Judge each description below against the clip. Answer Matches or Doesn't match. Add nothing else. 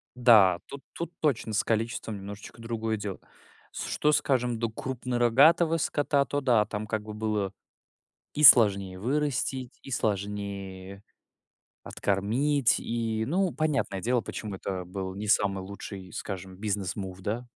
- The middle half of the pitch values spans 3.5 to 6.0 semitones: Matches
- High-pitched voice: Doesn't match